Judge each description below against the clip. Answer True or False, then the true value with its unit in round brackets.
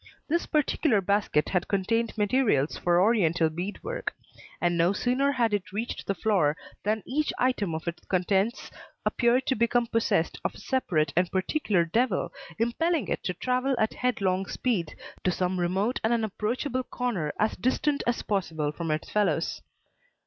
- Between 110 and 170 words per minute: True (160 wpm)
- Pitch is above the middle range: True (210 Hz)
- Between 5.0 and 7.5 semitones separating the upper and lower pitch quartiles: True (5.6 semitones)